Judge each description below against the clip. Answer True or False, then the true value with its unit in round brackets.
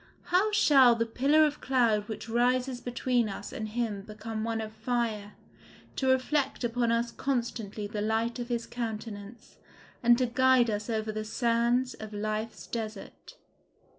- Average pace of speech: True (155 wpm)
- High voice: True (235 Hz)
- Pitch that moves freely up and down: False (2.4 semitones)